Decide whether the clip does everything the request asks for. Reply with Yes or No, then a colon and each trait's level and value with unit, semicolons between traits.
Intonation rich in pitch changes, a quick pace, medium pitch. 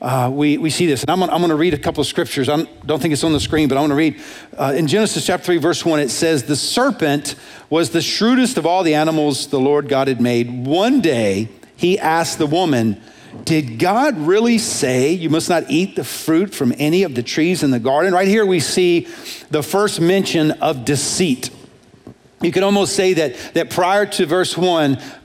No: average, 4.0 semitones; fast, 220 wpm; medium, 160 Hz